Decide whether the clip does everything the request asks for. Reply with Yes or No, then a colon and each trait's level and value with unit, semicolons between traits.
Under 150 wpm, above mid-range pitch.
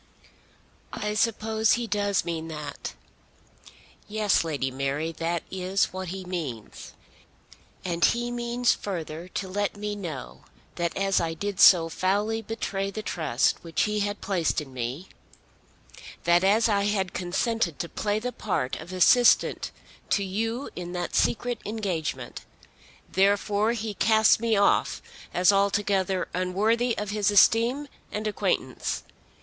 Yes: slow, 135 wpm; high, 195 Hz